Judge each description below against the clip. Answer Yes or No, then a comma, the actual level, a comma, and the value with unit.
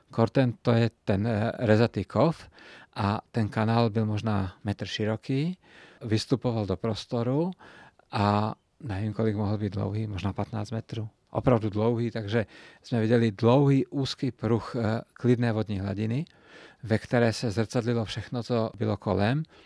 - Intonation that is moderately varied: No, narrow, 2.2 semitones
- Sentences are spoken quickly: No, average, 140 wpm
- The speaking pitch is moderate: No, low, 115 Hz